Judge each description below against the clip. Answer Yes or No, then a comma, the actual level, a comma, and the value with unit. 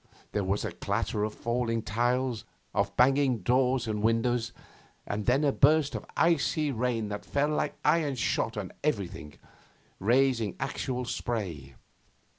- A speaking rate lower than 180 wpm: Yes, average, 140 wpm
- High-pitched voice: No, low, 120 Hz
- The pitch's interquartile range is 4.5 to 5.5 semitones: No, average, 4.1 semitones